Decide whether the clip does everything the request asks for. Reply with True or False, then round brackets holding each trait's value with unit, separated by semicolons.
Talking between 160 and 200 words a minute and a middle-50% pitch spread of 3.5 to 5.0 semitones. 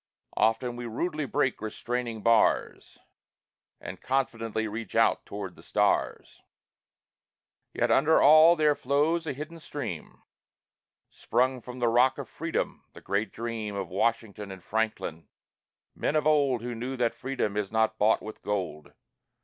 False (140 wpm; 4.2 semitones)